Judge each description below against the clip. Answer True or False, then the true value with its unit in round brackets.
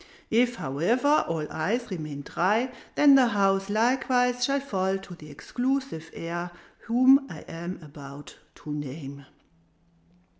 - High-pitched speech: True (195 Hz)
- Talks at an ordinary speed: False (125 wpm)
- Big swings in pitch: True (8.0 semitones)